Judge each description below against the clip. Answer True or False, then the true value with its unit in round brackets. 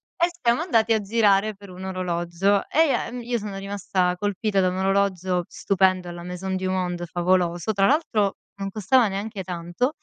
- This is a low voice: False (195 Hz)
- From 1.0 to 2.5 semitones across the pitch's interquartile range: False (2.9 semitones)